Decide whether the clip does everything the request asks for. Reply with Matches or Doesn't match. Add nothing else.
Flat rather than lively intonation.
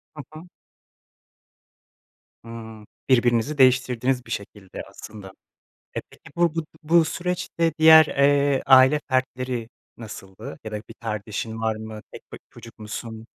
Doesn't match